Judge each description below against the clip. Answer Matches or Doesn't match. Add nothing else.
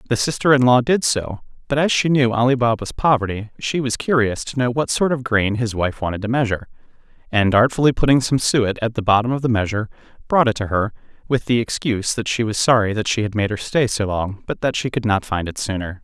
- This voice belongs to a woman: Doesn't match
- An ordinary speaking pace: Doesn't match